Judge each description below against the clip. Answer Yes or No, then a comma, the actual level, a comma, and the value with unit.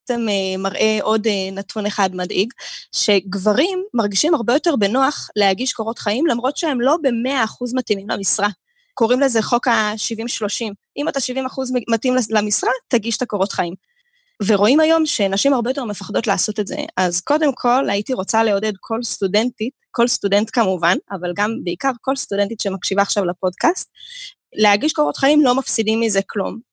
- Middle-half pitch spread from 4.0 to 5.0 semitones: Yes, average, 4.7 semitones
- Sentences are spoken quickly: Yes, fast, 155 wpm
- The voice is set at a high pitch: Yes, high, 225 Hz